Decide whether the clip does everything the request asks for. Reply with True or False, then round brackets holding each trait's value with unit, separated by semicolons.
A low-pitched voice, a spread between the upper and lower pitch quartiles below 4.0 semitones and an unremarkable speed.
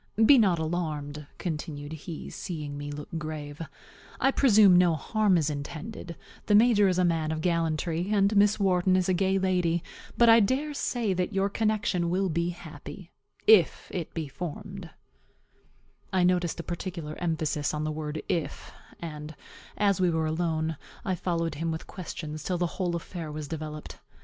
False (170 Hz; 3.4 semitones; 170 wpm)